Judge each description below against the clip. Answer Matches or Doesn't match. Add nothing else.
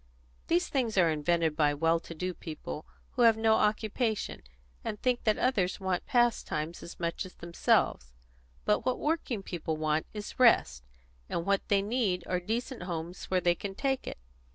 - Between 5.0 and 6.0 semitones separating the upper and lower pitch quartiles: Matches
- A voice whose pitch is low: Doesn't match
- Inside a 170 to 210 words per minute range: Matches